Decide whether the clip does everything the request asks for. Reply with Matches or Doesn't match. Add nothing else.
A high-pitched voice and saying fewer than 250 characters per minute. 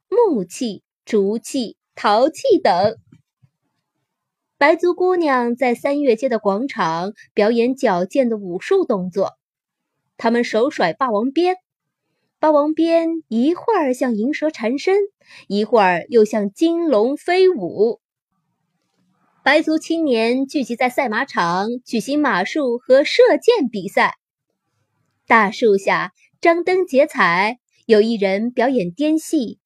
Matches